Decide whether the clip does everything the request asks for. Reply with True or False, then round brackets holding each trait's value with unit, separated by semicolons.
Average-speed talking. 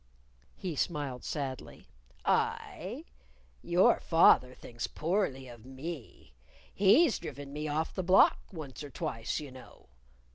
False (120 wpm)